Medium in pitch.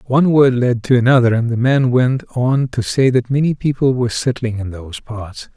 No: low, 120 Hz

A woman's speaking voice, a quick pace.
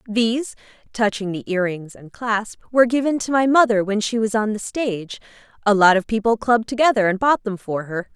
Yes: female; fast, 215 wpm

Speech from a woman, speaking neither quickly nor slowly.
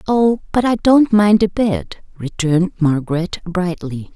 Yes: female; average, 145 wpm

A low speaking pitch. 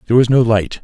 Yes: low, 115 Hz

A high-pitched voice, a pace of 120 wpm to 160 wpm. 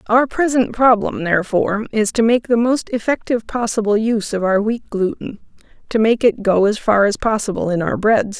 No: high, 220 Hz; average, 195 wpm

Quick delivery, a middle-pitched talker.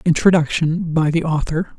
No: slow, 135 wpm; medium, 160 Hz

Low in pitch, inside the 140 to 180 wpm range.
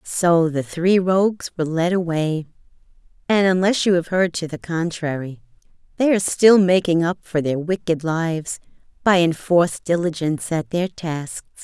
No: medium, 170 Hz; average, 155 wpm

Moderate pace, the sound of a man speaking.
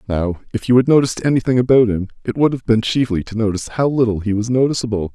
No: fast, 235 wpm; male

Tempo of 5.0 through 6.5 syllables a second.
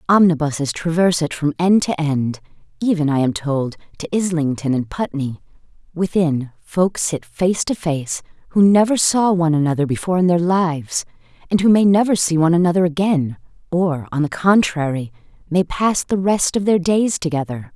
Yes: 5.2 syllables/s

